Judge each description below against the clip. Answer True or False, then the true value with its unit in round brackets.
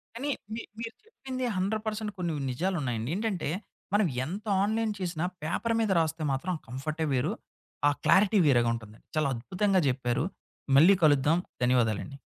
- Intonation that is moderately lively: False (7.8 semitones)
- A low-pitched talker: False (170 Hz)